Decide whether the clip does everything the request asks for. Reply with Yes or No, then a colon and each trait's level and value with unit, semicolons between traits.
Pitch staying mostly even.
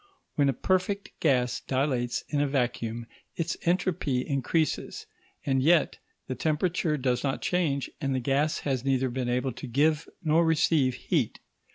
No: average, 3.6 semitones